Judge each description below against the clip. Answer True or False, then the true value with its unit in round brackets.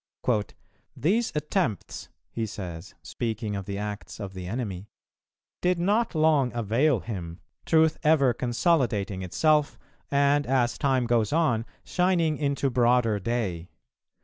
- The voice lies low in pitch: True (120 Hz)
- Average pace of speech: False (120 wpm)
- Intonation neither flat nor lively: False (6.7 semitones)